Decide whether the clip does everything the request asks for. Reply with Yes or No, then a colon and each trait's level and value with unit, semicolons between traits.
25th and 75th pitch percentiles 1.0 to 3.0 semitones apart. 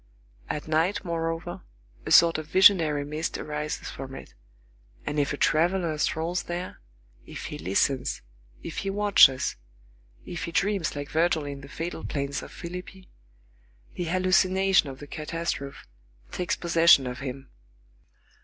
No: average, 3.6 semitones